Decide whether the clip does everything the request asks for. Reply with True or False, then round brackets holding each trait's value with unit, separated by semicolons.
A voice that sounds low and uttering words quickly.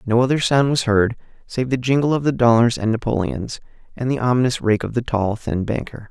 True (120 Hz; 215 wpm)